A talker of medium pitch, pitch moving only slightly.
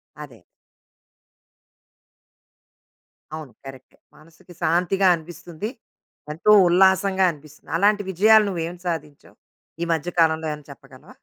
No: medium, 170 Hz; average, 3.6 semitones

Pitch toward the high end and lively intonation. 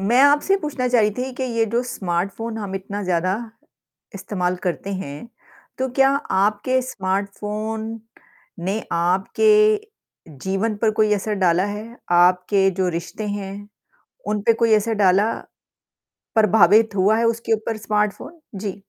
No: high, 210 Hz; average, 3.1 semitones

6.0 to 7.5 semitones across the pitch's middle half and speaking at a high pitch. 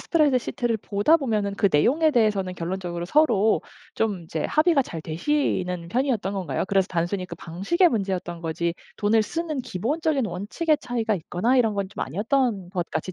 Yes: wide, 6.5 semitones; high, 205 Hz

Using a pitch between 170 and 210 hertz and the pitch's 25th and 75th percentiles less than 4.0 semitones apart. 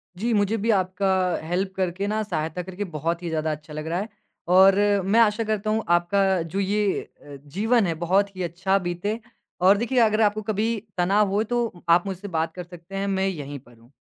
Yes: high, 190 Hz; average, 3.2 semitones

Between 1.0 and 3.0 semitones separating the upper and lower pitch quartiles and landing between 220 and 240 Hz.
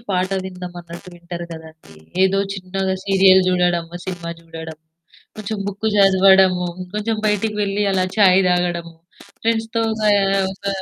No: narrow, 2.4 semitones; medium, 185 Hz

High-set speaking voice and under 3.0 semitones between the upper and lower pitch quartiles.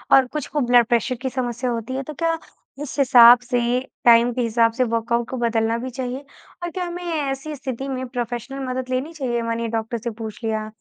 Yes: high, 245 Hz; narrow, 2.5 semitones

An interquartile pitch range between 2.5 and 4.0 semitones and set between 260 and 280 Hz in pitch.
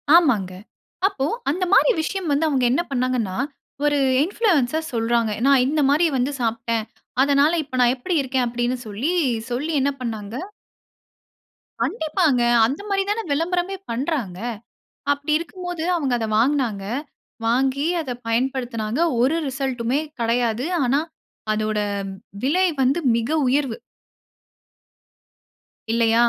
No: average, 4.8 semitones; very high, 265 Hz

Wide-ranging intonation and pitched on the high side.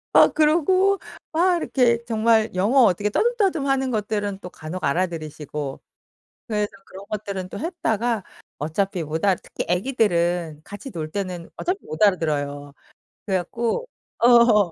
Yes: wide, 6.2 semitones; high, 205 Hz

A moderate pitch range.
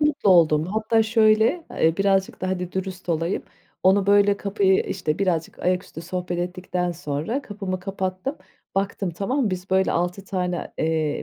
No: narrow, 2.3 semitones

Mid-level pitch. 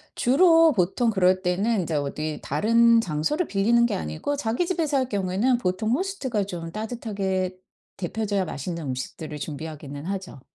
No: high, 195 Hz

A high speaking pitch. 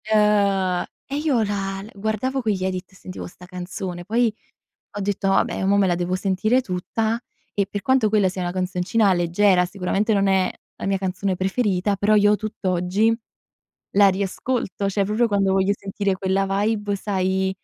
Yes: high, 195 Hz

